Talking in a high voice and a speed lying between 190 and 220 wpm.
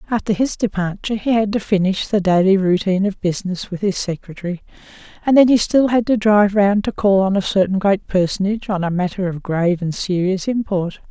Yes: high, 195 Hz; fast, 205 wpm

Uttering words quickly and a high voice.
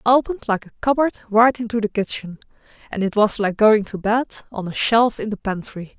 Yes: fast, 220 wpm; high, 220 Hz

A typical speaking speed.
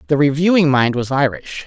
Yes: average, 180 wpm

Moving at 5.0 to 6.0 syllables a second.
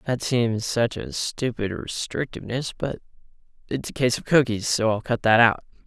No: 4.8 syllables/s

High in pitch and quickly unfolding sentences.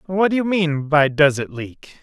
No: medium, 160 Hz; fast, 235 wpm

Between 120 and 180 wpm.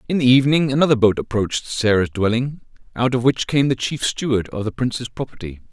No: average, 200 wpm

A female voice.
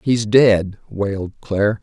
No: male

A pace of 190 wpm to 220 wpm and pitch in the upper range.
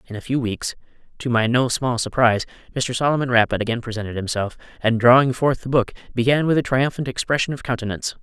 No: average, 195 wpm; low, 120 Hz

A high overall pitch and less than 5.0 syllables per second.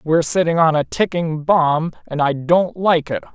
No: medium, 160 Hz; 4.6 syllables/s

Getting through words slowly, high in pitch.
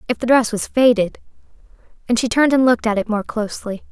No: average, 200 wpm; high, 230 Hz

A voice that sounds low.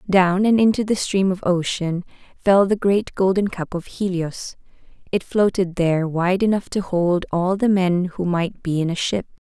No: medium, 185 Hz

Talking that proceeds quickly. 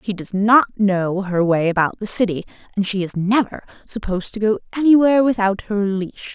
No: average, 190 wpm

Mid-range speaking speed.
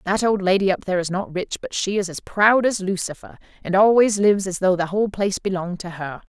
No: fast, 245 wpm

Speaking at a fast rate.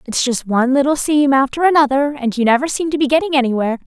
Yes: fast, 225 wpm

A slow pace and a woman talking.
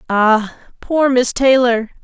Yes: slow, 120 wpm; female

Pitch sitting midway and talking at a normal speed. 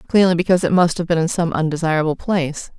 No: medium, 170 Hz; fast, 215 wpm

